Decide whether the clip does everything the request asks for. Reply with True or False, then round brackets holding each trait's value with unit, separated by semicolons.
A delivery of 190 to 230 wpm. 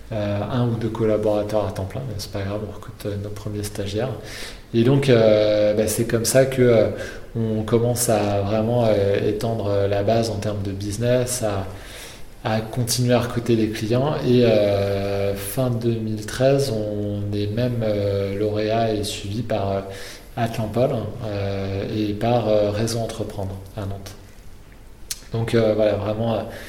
False (165 wpm)